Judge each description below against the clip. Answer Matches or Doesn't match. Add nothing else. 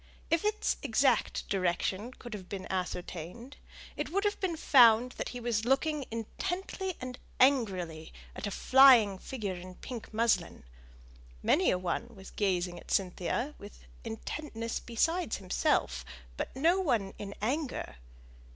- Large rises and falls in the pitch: Matches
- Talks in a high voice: Matches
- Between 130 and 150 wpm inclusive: Matches